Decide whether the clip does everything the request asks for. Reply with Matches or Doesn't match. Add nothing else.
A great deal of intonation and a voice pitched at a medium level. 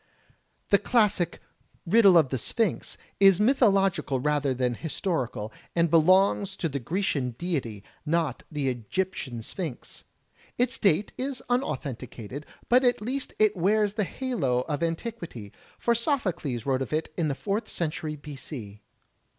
Matches